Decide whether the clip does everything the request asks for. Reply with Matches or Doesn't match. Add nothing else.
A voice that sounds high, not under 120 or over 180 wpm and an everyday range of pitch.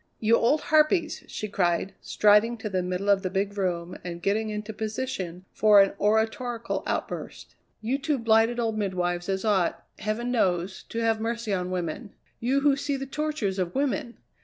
Matches